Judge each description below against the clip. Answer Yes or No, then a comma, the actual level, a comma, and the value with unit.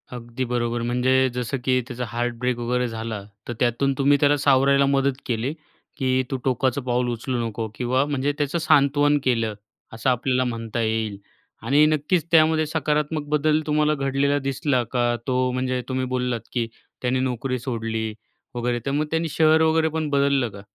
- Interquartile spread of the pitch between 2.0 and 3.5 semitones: Yes, average, 3.1 semitones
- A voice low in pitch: Yes, low, 130 Hz